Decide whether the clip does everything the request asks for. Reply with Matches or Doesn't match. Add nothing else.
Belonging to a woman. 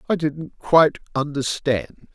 Doesn't match